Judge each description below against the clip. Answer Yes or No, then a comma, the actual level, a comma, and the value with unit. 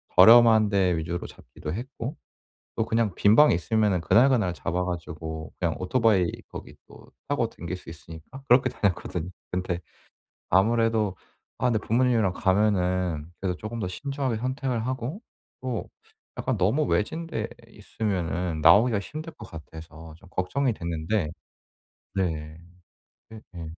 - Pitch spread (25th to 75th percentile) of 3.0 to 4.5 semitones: No, average, 5.1 semitones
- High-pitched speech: No, low, 100 Hz